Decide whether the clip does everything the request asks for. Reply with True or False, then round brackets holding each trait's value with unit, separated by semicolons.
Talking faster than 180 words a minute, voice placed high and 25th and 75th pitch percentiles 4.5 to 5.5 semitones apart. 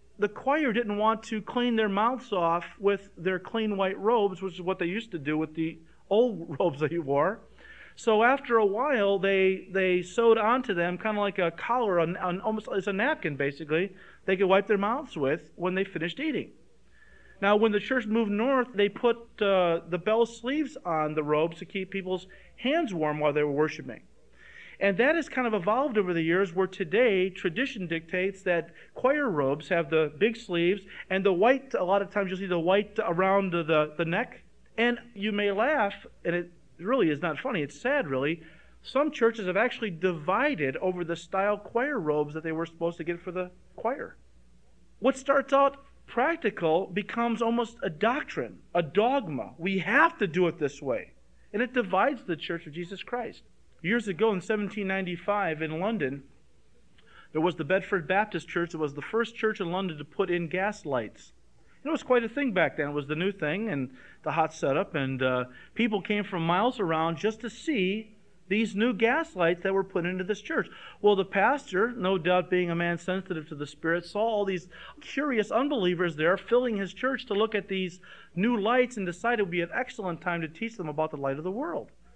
True (205 wpm; 195 Hz; 4.8 semitones)